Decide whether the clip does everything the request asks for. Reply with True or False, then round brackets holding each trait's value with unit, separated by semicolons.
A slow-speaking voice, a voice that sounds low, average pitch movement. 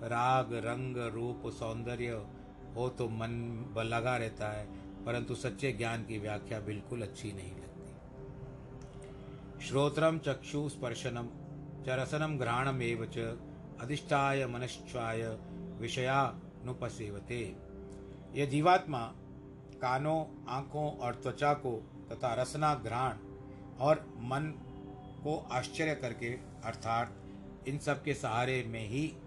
True (105 wpm; 125 Hz; 3.8 semitones)